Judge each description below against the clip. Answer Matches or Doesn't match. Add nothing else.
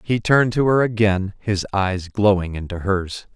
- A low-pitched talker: Matches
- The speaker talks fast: Doesn't match